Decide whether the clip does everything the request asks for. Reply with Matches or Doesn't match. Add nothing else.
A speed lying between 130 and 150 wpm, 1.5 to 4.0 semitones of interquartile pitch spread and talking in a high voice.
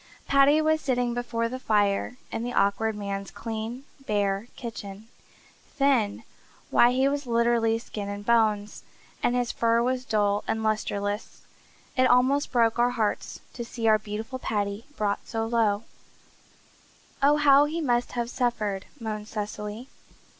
Matches